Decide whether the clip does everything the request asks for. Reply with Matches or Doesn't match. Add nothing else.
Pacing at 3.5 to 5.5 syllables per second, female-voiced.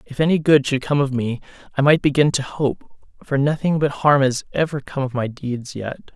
Doesn't match